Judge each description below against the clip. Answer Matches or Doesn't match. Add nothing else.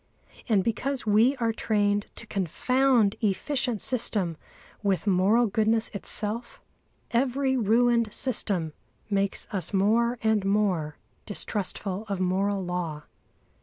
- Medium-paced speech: Doesn't match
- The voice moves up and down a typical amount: Matches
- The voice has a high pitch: Matches